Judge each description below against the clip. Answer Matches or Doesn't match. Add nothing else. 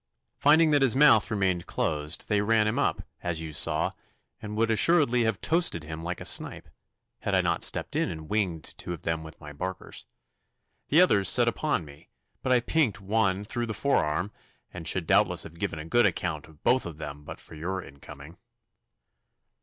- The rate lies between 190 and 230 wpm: Matches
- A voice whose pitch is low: Matches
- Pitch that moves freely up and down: Matches